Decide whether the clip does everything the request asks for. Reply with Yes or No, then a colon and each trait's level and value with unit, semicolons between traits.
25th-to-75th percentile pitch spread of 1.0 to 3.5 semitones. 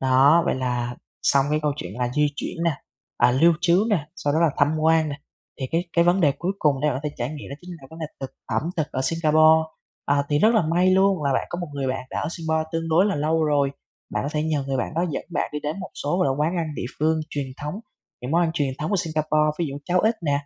Yes: average, 3.0 semitones